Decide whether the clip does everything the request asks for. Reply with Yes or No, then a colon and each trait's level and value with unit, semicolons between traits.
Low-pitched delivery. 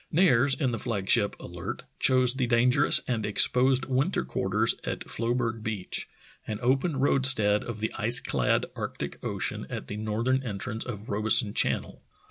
Yes: low, 120 Hz